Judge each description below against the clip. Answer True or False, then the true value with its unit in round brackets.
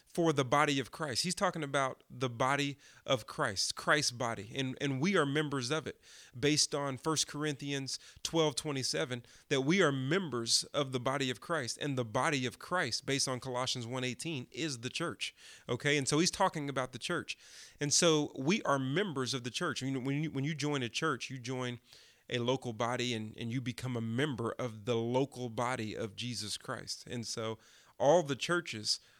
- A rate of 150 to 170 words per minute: False (195 wpm)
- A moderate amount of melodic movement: True (3.3 semitones)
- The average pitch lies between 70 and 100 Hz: False (135 Hz)